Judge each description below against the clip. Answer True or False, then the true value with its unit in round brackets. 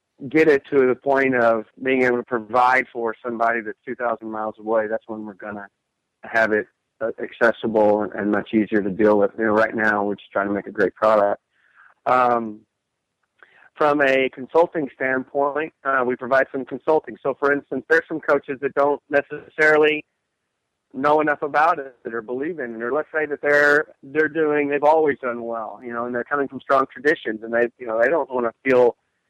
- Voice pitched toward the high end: False (125 Hz)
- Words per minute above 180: True (195 wpm)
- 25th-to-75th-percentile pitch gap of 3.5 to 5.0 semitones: True (4.3 semitones)